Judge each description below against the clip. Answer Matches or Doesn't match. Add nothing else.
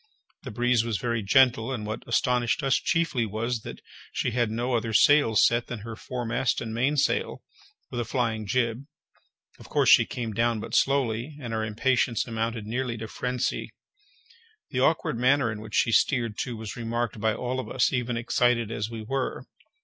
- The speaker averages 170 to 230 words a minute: Matches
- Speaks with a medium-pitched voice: Doesn't match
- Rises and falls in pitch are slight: Matches